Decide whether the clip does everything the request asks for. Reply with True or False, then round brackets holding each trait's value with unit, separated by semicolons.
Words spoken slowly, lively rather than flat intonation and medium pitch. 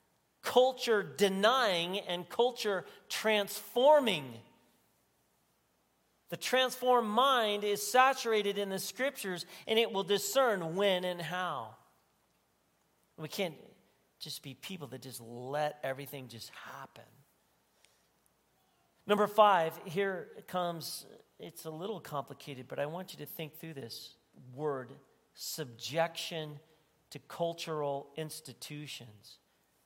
True (105 wpm; 5.9 semitones; 170 Hz)